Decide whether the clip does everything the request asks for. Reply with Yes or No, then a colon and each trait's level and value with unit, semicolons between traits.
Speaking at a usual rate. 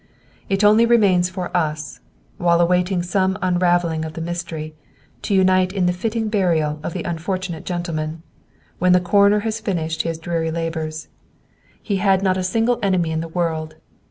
Yes: average, 165 wpm